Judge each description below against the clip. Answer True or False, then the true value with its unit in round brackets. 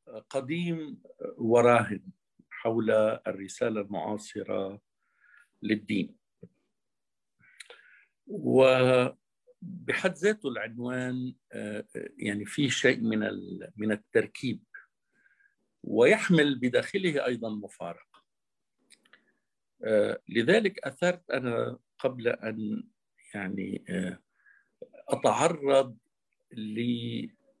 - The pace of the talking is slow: True (60 wpm)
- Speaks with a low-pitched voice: True (130 Hz)